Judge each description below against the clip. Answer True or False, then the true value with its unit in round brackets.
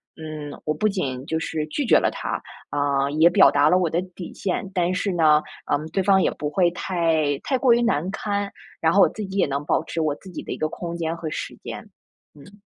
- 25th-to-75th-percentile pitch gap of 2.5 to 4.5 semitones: True (4.0 semitones)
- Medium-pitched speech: True (165 Hz)